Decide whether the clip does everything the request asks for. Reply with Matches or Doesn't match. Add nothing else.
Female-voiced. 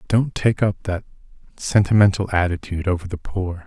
Doesn't match